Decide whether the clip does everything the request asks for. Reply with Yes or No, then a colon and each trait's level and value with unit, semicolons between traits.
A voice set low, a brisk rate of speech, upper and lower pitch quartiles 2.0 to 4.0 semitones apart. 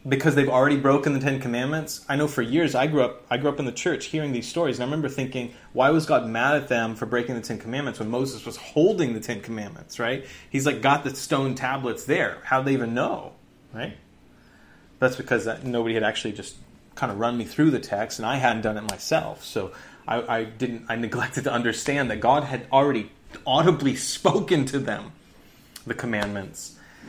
Yes: low, 130 Hz; fast, 215 wpm; average, 3.3 semitones